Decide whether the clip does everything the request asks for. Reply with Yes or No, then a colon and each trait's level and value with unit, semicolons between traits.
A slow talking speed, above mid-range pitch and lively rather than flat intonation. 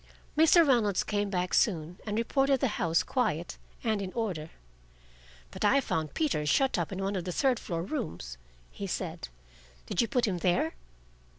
No: average, 175 wpm; high, 200 Hz; wide, 6.3 semitones